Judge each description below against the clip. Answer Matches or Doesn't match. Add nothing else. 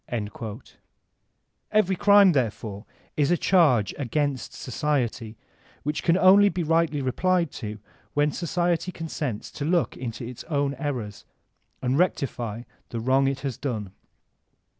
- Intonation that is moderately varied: Doesn't match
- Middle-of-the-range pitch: Matches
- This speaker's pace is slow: Matches